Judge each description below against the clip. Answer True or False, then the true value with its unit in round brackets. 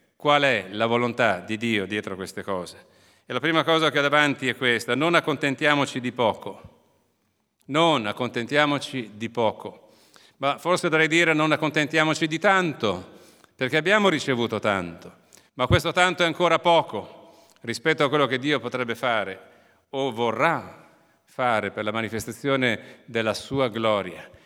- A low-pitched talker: True (130 Hz)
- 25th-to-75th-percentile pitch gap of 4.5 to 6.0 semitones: True (5.3 semitones)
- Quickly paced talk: False (145 wpm)